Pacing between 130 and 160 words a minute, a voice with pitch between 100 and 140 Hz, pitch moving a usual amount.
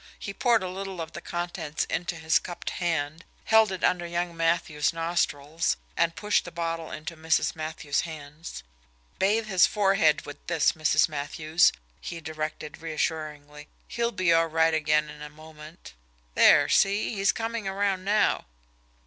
No: average, 155 wpm; medium, 165 Hz; average, 3.1 semitones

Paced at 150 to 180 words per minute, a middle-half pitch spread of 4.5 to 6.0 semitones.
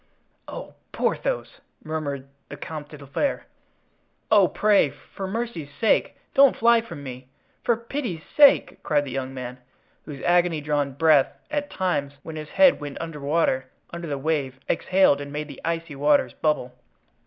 Yes: average, 160 wpm; average, 4.9 semitones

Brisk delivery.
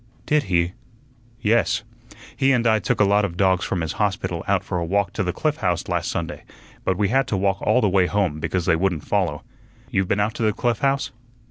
Yes: fast, 230 wpm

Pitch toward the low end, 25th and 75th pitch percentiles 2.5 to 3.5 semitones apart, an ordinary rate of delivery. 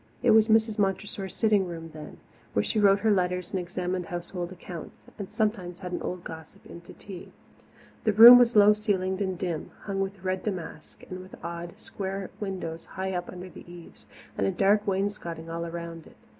No: medium, 185 Hz; average, 2.8 semitones; average, 195 wpm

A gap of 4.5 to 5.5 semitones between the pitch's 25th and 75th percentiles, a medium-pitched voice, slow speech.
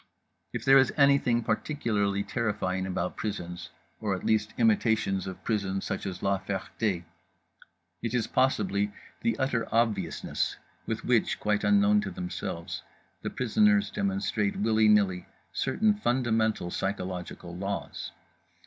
No: average, 4.9 semitones; low, 105 Hz; slow, 125 wpm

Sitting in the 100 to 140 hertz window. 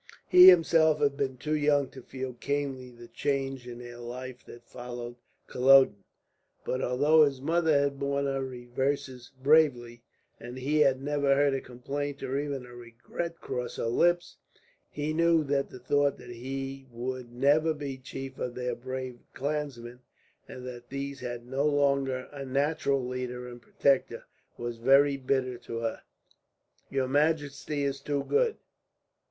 Yes: low, 135 Hz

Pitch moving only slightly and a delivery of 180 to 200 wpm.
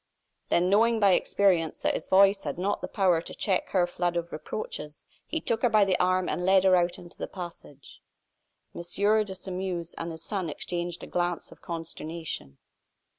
Yes: narrow, 2.3 semitones; average, 185 wpm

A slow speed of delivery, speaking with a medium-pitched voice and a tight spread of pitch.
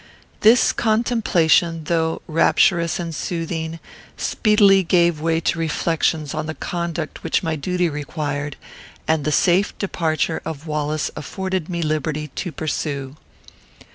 Yes: slow, 125 wpm; medium, 165 Hz; narrow, 2.3 semitones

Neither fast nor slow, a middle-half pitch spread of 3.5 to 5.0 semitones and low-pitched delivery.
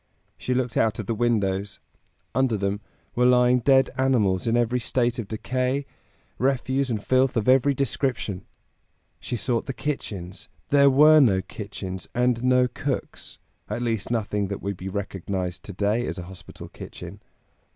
Yes: average, 160 wpm; average, 4.2 semitones; low, 120 Hz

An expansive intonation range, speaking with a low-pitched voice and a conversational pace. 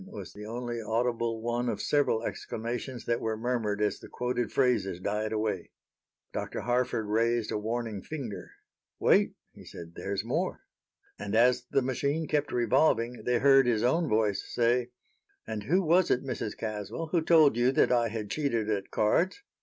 No: average, 2.7 semitones; low, 120 Hz; average, 170 wpm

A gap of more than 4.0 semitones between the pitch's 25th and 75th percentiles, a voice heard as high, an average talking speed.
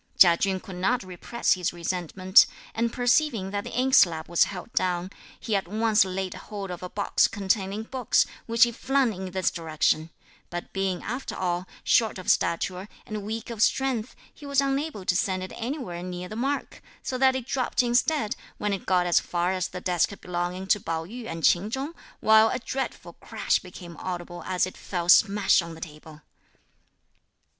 Yes: average, 4.4 semitones; high, 195 Hz; average, 185 wpm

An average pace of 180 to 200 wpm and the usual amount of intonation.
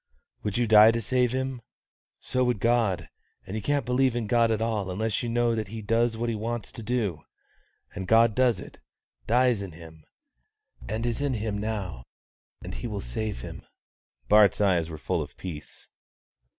Yes: average, 185 wpm; average, 3.1 semitones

